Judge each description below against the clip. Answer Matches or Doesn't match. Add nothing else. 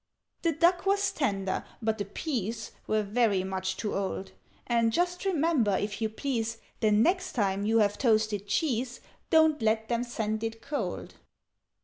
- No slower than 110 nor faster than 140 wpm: Doesn't match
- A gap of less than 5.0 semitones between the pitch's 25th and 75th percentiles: Doesn't match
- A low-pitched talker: Doesn't match